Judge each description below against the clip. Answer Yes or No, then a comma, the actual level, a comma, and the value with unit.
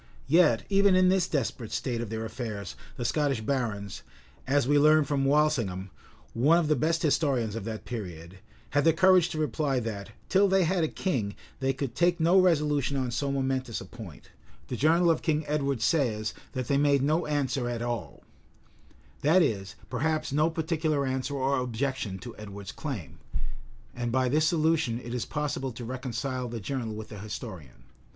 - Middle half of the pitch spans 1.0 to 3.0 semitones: No, average, 5.0 semitones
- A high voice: No, low, 135 Hz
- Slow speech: No, average, 180 wpm